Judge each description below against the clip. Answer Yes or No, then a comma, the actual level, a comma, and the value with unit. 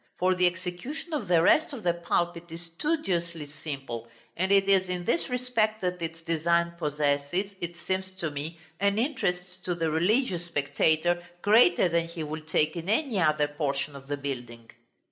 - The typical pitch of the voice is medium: Yes, medium, 170 Hz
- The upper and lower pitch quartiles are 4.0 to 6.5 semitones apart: No, average, 3.3 semitones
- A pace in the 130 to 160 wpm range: No, average, 175 wpm